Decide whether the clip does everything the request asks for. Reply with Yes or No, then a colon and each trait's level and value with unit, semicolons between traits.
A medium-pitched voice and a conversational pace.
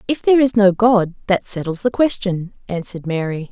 No: high, 200 Hz; average, 190 wpm